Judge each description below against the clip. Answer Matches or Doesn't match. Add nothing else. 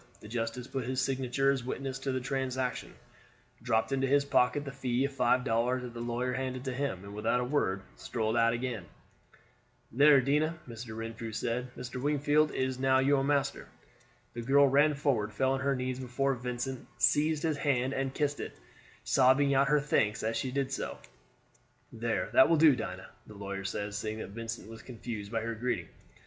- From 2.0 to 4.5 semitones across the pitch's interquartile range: Matches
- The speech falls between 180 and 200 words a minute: Matches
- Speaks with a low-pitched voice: Matches